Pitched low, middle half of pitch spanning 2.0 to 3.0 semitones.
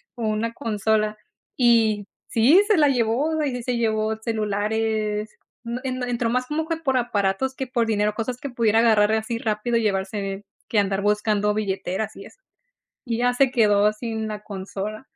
No: high, 220 Hz; average, 2.7 semitones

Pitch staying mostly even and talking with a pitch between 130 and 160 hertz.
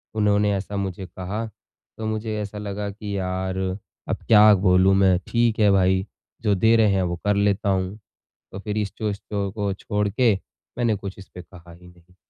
No: narrow, 2.0 semitones; low, 100 Hz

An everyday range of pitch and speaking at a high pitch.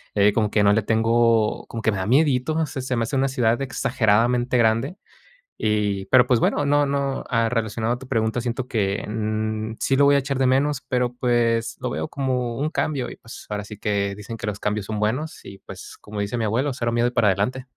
No: average, 3.4 semitones; low, 115 Hz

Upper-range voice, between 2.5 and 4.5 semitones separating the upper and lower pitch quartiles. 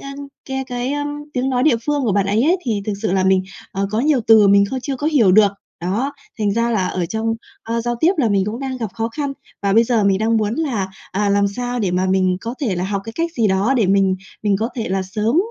Yes: high, 220 Hz; average, 4.2 semitones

